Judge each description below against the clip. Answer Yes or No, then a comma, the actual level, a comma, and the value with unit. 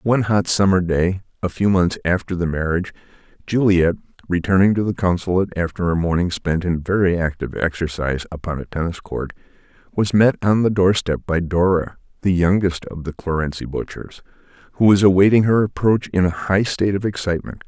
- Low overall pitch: Yes, very low, 90 Hz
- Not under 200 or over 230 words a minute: No, average, 175 wpm